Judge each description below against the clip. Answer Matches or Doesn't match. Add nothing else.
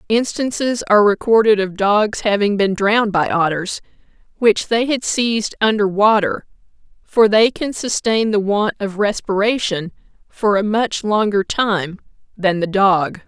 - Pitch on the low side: Doesn't match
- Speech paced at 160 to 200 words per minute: Doesn't match